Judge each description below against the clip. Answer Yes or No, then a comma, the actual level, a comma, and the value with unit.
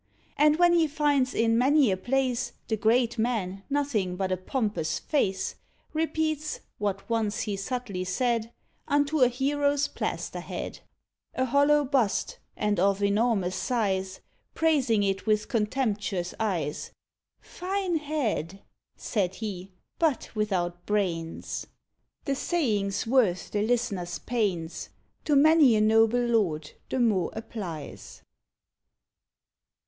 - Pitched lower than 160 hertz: No, high, 225 Hz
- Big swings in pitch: Yes, wide, 5.9 semitones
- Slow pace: Yes, slow, 120 wpm